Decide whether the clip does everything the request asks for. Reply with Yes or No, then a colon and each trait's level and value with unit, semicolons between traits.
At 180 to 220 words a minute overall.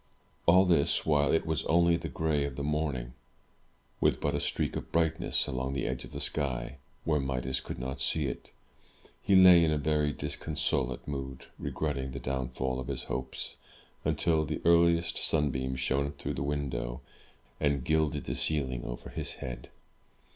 No: average, 170 wpm